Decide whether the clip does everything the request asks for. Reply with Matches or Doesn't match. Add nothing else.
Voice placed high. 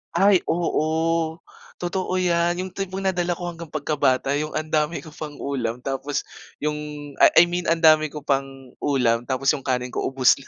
Doesn't match